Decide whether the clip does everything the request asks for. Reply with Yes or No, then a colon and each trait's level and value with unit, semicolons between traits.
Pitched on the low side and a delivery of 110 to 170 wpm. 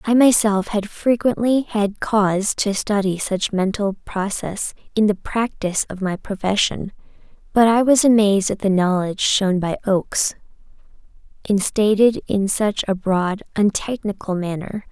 No: high, 205 Hz; average, 140 wpm